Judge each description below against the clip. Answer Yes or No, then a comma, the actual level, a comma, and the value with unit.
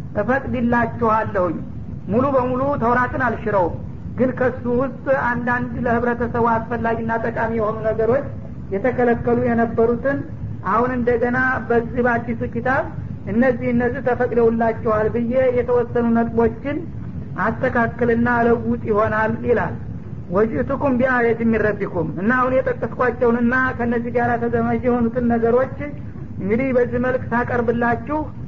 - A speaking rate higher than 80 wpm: Yes, average, 95 wpm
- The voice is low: No, high, 235 Hz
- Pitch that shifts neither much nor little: No, narrow, 1.4 semitones